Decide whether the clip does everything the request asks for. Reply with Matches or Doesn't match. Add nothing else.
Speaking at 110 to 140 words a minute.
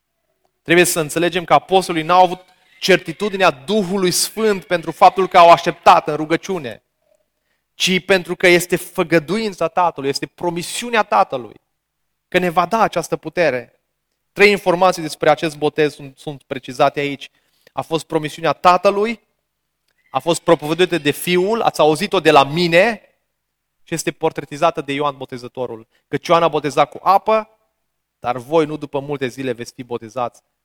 Doesn't match